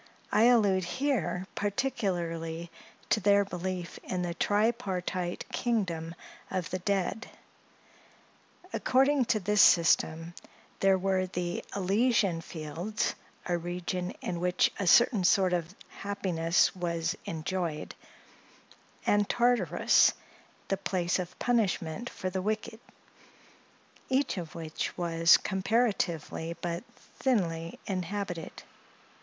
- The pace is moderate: No, slow, 105 wpm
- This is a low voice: No, medium, 185 Hz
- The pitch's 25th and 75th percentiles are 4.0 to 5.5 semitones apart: No, average, 3.3 semitones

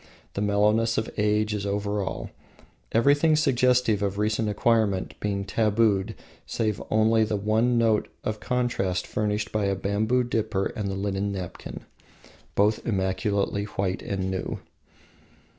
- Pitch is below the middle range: Yes, low, 105 Hz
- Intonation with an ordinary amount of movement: No, narrow, 2.0 semitones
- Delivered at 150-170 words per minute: No, slow, 135 wpm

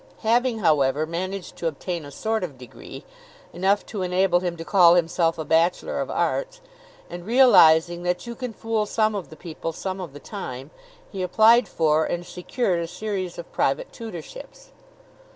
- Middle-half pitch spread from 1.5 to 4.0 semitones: No, average, 4.8 semitones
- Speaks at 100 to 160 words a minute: No, average, 170 wpm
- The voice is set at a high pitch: No, medium, 180 Hz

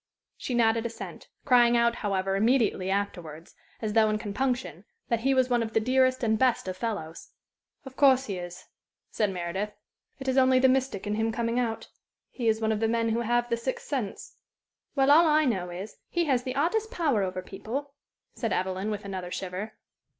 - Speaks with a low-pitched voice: No, high, 230 Hz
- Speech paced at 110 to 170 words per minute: No, average, 195 wpm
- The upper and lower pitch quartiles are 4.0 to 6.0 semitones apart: Yes, average, 4.3 semitones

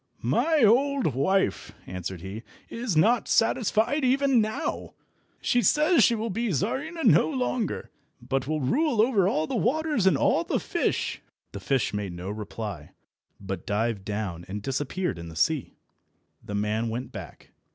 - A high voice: No, medium, 160 Hz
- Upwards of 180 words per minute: No, average, 155 wpm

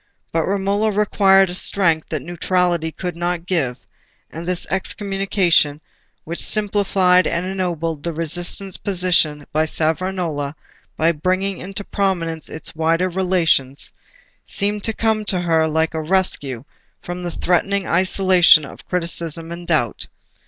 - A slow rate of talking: Yes, slow, 130 wpm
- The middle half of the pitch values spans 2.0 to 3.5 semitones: Yes, average, 3.0 semitones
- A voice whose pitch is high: No, medium, 175 Hz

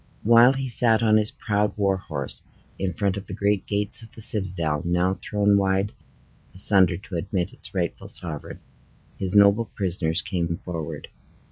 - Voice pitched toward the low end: Yes, low, 100 Hz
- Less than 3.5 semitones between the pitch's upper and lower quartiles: Yes, average, 2.8 semitones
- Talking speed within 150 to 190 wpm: Yes, average, 160 wpm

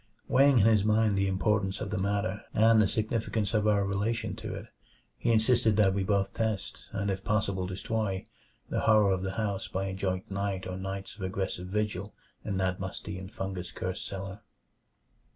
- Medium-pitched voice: No, low, 100 Hz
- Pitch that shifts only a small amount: Yes, narrow, 2.1 semitones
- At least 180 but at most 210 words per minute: Yes, average, 190 wpm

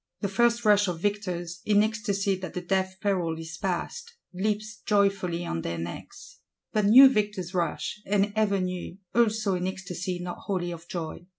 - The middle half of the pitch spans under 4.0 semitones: Yes, average, 3.1 semitones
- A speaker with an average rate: Yes, average, 170 wpm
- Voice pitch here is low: No, high, 190 Hz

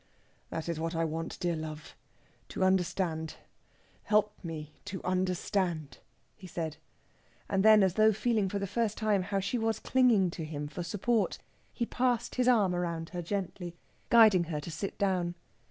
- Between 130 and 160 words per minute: No, average, 170 wpm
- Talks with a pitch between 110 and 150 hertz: No, medium, 185 Hz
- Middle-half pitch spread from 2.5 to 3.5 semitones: No, average, 4.1 semitones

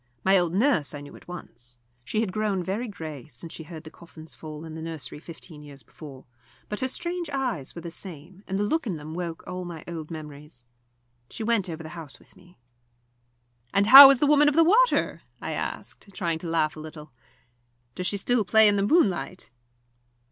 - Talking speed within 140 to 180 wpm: No, fast, 205 wpm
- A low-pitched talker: No, medium, 175 Hz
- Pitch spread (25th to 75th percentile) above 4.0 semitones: Yes, average, 5.2 semitones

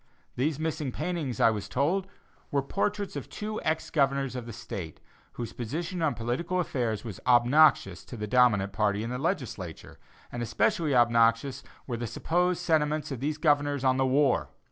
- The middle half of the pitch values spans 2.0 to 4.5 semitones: No, average, 5.0 semitones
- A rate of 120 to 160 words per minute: No, average, 170 wpm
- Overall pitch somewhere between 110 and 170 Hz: Yes, low, 135 Hz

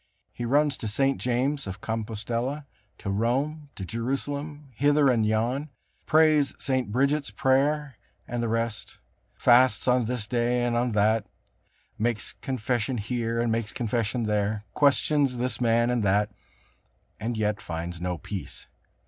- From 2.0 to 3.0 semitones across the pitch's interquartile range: No, average, 3.7 semitones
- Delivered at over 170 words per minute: No, average, 140 wpm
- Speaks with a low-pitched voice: Yes, low, 120 Hz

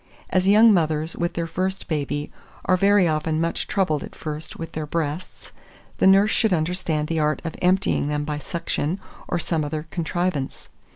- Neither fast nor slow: Yes, average, 175 wpm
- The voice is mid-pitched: Yes, medium, 165 Hz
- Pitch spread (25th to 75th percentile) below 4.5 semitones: Yes, average, 3.2 semitones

